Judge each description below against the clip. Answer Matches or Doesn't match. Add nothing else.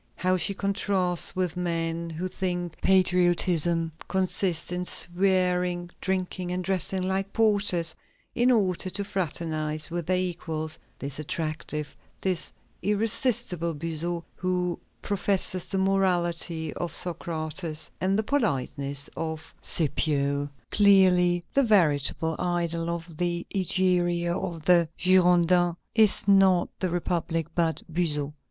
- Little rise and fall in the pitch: Matches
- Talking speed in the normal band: Doesn't match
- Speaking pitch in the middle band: Matches